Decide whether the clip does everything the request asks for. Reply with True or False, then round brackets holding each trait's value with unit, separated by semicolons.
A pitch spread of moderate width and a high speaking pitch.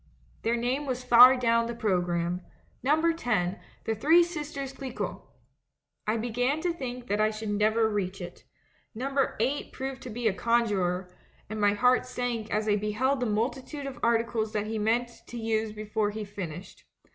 True (3.2 semitones; 230 Hz)